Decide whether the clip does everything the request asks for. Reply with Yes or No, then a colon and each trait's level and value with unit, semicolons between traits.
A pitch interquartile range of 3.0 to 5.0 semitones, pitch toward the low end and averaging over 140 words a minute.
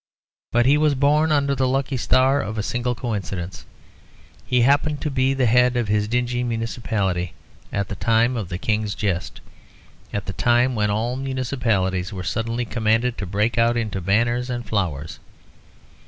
Yes: average, 3.7 semitones; low, 115 Hz; average, 170 wpm